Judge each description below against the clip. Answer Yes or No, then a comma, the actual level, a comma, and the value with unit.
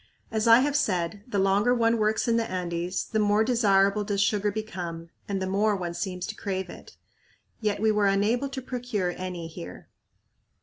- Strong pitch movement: No, average, 3.0 semitones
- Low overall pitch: No, high, 205 Hz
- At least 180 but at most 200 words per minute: Yes, average, 185 wpm